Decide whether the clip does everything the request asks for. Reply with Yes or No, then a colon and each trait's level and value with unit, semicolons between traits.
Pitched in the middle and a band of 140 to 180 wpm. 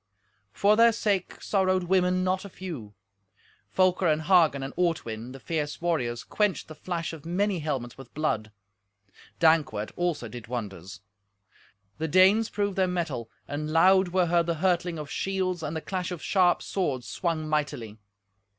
Yes: medium, 170 Hz; average, 160 wpm